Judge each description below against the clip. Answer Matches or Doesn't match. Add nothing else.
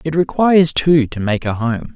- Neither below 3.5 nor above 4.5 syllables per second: Doesn't match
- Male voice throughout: Matches